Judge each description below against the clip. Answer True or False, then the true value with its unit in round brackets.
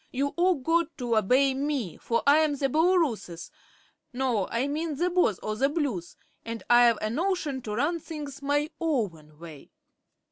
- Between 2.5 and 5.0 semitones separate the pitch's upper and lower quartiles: False (5.4 semitones)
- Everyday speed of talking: True (165 wpm)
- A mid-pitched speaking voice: False (275 Hz)